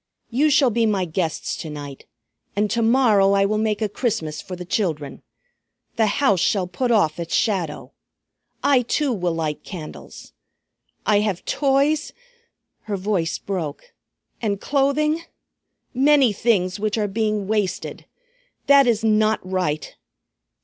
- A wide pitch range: No, average, 4.7 semitones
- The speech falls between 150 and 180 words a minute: No, average, 140 wpm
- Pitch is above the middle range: Yes, high, 210 Hz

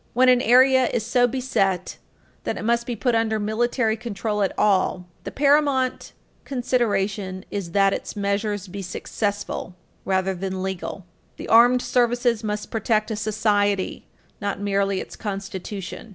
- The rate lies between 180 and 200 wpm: No, average, 145 wpm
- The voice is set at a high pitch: Yes, high, 210 Hz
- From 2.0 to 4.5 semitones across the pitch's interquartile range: Yes, average, 3.5 semitones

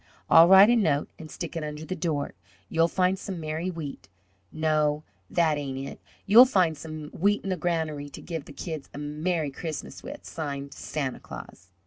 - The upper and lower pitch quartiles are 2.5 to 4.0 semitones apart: Yes, average, 3.3 semitones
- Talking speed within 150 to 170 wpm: No, average, 185 wpm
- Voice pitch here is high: No, medium, 160 Hz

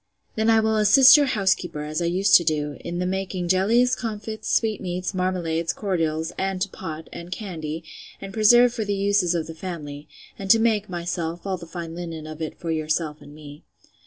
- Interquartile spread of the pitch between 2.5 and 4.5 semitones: Yes, average, 4.1 semitones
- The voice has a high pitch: No, medium, 180 Hz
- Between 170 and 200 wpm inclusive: Yes, average, 195 wpm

